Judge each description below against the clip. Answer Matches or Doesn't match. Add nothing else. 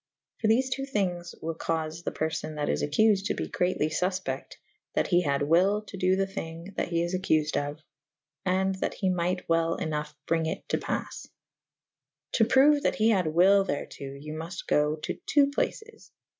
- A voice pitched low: Doesn't match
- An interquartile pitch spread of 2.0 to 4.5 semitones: Matches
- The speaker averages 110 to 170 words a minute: Doesn't match